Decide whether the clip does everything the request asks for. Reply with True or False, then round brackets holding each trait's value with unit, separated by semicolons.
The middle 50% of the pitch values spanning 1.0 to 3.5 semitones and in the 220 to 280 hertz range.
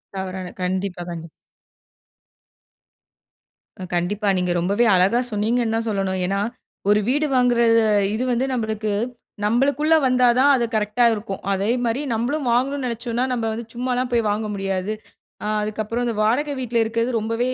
True (3.2 semitones; 230 Hz)